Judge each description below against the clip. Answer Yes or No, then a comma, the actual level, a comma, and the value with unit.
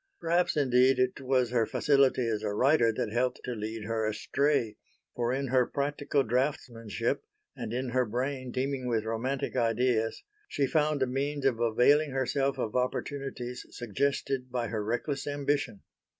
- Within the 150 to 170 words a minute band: Yes, average, 155 wpm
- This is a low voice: Yes, low, 125 Hz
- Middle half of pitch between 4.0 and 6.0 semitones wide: No, average, 3.0 semitones